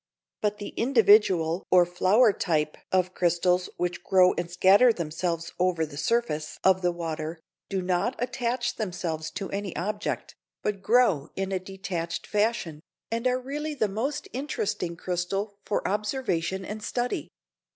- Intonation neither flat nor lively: Yes, average, 3.8 semitones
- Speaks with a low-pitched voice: No, high, 190 Hz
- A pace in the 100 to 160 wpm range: Yes, average, 145 wpm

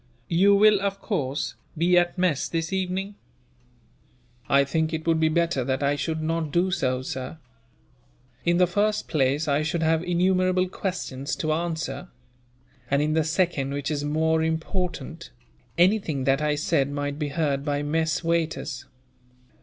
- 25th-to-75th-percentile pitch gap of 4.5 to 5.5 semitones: No, average, 3.5 semitones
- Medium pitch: Yes, medium, 160 Hz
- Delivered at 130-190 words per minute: Yes, average, 155 wpm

